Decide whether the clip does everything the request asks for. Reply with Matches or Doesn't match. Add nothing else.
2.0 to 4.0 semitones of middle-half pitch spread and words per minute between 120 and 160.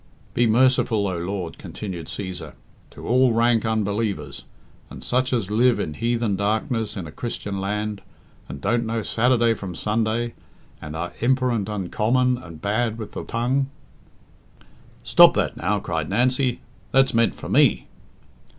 Matches